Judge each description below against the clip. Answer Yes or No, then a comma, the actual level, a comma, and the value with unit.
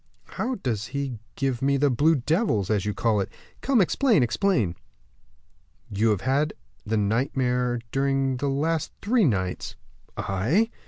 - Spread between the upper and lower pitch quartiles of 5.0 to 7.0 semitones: Yes, wide, 5.6 semitones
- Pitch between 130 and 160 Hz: Yes, low, 135 Hz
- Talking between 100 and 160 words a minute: Yes, average, 145 wpm